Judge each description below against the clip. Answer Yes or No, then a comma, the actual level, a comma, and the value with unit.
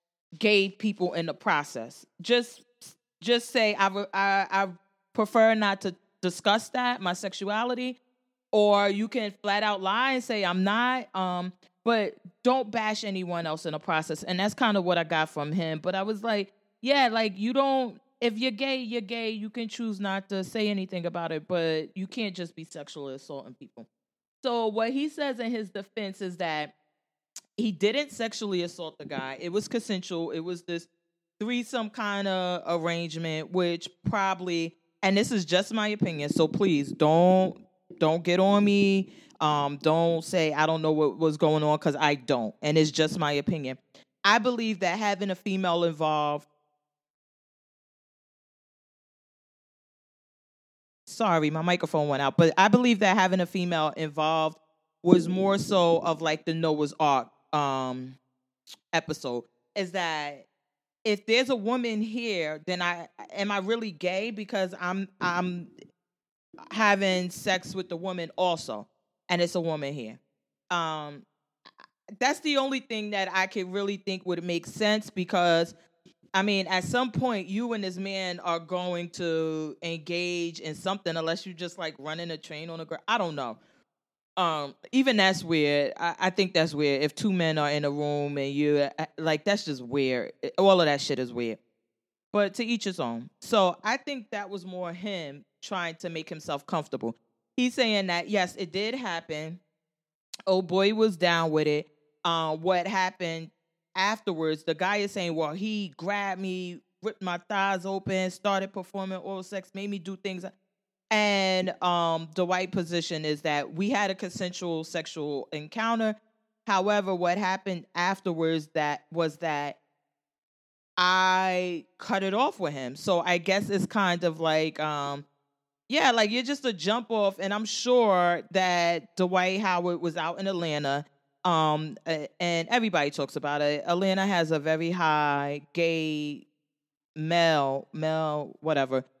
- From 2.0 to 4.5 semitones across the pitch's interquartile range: Yes, average, 4.2 semitones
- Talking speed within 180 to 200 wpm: No, average, 165 wpm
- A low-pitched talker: No, medium, 180 Hz